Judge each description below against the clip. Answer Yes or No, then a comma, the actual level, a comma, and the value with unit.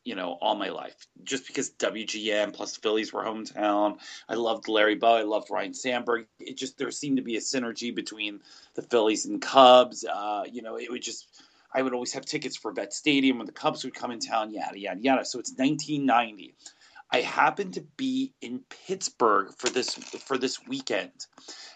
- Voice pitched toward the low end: Yes, low, 125 Hz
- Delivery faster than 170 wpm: Yes, average, 200 wpm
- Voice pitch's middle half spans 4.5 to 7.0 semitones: Yes, average, 5.3 semitones